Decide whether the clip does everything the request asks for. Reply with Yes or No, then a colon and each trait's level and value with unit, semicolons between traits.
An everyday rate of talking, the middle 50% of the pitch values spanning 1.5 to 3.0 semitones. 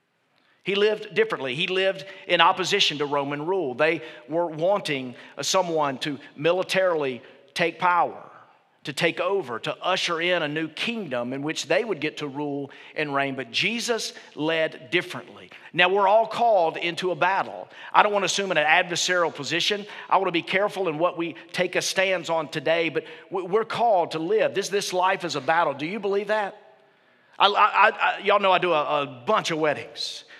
No: average, 190 wpm; average, 4.1 semitones